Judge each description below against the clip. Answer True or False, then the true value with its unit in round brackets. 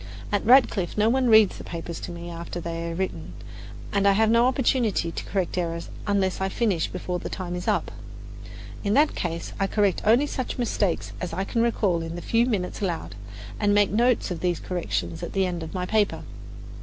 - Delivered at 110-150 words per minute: False (205 wpm)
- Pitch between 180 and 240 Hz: True (190 Hz)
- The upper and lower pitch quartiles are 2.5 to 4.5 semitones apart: True (4.1 semitones)